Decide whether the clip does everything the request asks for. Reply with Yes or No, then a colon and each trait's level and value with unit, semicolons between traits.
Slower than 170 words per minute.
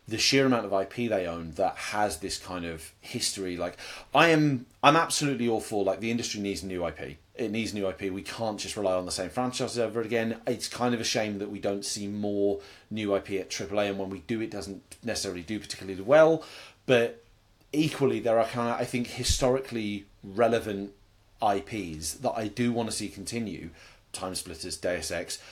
No: average, 200 wpm